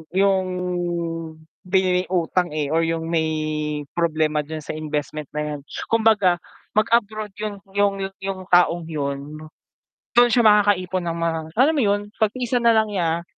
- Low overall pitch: No, medium, 180 Hz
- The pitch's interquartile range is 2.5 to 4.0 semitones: No, average, 4.8 semitones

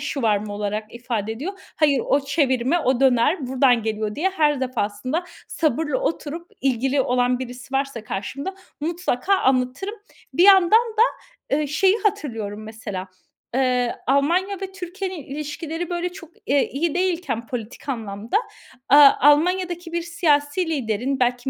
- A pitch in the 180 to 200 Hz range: No, very high, 275 Hz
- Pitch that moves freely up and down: Yes, wide, 5.8 semitones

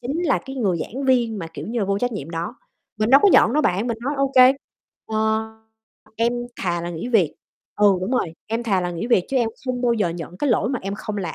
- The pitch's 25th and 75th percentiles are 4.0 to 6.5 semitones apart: Yes, average, 5.3 semitones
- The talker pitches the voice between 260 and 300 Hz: No, high, 220 Hz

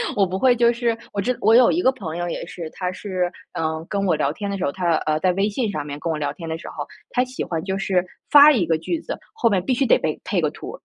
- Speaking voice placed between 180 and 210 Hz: Yes, high, 190 Hz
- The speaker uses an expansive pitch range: Yes, wide, 6.1 semitones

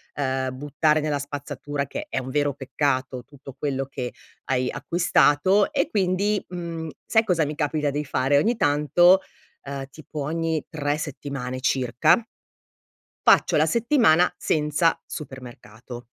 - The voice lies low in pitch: No, medium, 145 Hz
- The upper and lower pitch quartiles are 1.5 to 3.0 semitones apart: No, average, 3.5 semitones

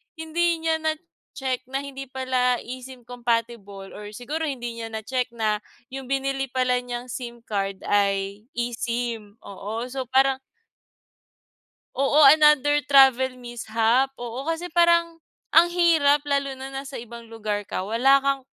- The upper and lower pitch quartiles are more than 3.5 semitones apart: No, average, 3.1 semitones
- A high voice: Yes, very high, 255 Hz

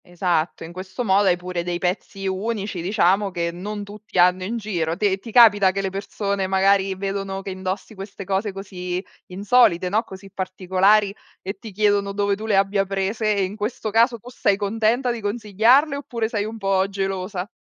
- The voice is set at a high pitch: Yes, high, 195 Hz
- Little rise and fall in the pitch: Yes, narrow, 2.0 semitones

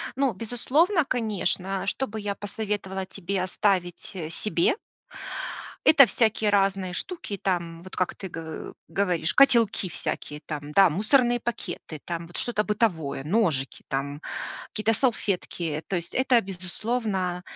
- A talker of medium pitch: No, high, 195 Hz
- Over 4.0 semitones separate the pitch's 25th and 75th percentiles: Yes, average, 4.5 semitones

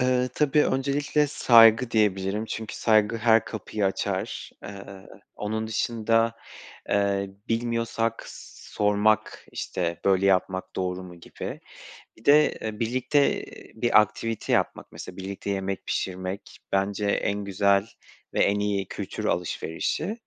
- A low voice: Yes, low, 105 Hz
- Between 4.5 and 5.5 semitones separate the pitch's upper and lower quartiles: No, average, 2.8 semitones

